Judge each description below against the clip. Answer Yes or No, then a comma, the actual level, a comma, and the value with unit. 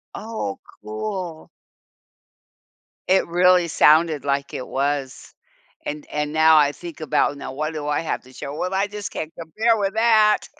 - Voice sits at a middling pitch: Yes, medium, 160 Hz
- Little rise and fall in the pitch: No, average, 4.7 semitones